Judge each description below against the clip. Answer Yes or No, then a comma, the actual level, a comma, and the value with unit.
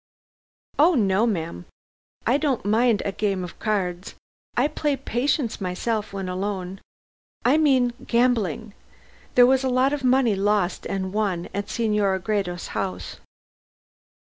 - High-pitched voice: Yes, high, 210 Hz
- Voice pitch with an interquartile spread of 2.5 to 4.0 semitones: No, average, 4.6 semitones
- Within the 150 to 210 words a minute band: No, slow, 135 wpm